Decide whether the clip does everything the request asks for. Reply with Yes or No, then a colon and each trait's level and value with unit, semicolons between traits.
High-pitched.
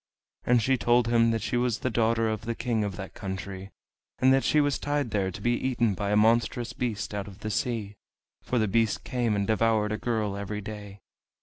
No: low, 110 Hz